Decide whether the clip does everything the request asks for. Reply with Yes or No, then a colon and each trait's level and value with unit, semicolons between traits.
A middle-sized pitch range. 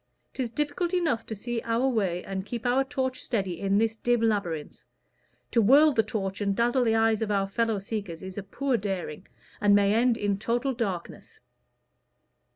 Yes: average, 3.6 semitones